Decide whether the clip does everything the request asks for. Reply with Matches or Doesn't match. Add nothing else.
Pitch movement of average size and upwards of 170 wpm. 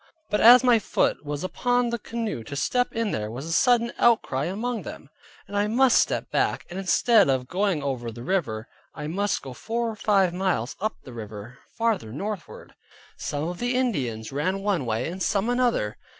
Doesn't match